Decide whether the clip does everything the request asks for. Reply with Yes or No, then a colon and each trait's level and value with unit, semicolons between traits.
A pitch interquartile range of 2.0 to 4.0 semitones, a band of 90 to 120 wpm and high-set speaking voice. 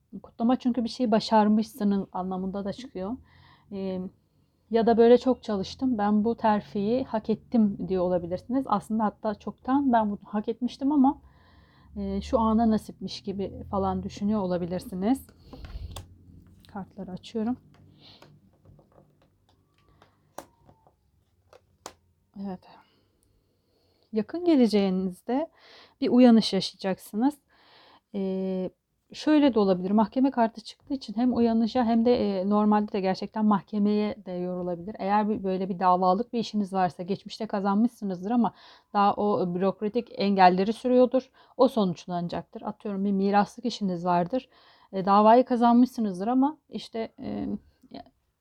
Yes: average, 3.6 semitones; average, 115 wpm; high, 210 Hz